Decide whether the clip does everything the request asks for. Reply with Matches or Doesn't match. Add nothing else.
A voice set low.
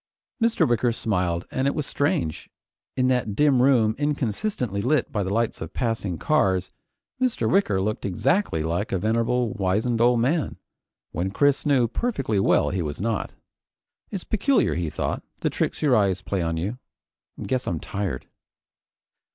Matches